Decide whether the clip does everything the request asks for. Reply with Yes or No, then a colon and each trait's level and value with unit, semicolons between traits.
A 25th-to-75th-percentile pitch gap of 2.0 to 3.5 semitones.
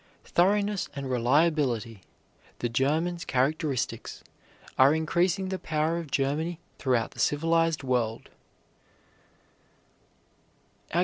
No: average, 4.5 semitones